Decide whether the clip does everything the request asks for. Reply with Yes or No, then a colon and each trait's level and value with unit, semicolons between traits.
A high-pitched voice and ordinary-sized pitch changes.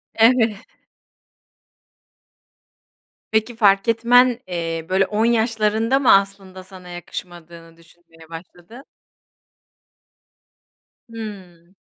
Yes: high, 195 Hz; average, 4.6 semitones